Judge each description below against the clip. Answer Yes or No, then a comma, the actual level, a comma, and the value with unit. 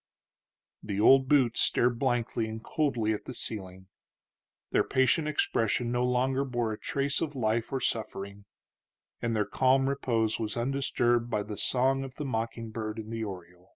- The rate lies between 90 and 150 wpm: No, average, 165 wpm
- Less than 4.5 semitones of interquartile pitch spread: Yes, average, 3.4 semitones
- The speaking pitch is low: Yes, low, 120 Hz